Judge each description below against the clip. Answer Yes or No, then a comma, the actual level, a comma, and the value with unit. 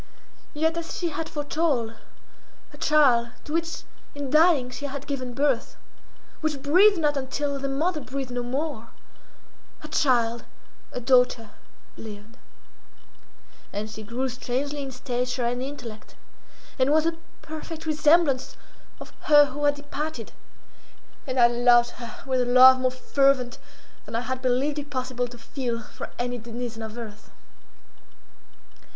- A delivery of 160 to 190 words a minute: No, average, 145 wpm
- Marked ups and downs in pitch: No, average, 3.3 semitones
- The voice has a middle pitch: No, very high, 260 Hz